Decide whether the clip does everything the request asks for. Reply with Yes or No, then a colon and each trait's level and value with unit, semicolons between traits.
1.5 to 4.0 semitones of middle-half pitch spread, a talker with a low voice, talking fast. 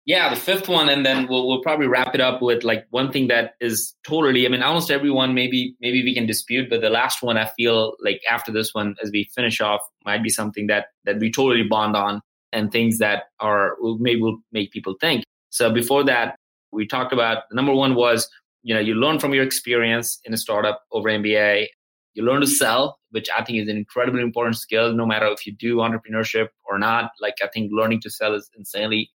Yes: average, 2.8 semitones; low, 115 Hz; fast, 220 wpm